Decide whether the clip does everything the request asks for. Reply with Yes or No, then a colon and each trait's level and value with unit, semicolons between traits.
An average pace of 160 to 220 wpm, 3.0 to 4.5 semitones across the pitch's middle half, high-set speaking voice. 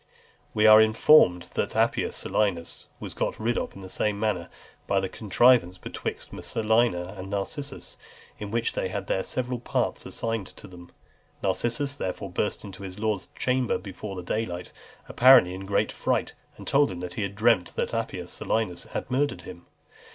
No: average, 165 wpm; average, 3.9 semitones; low, 105 Hz